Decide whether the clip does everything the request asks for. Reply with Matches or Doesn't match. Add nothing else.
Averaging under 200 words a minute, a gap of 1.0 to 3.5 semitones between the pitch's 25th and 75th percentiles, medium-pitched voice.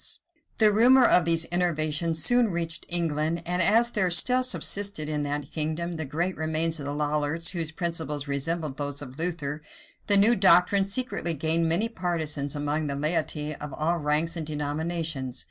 Matches